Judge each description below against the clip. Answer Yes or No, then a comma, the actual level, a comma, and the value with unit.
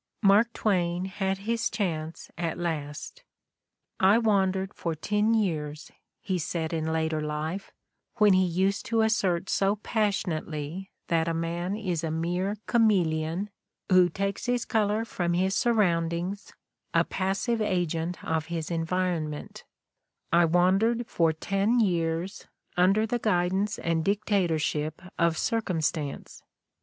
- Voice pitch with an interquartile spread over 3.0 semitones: Yes, average, 3.8 semitones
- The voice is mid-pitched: Yes, medium, 180 Hz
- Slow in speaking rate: Yes, slow, 125 wpm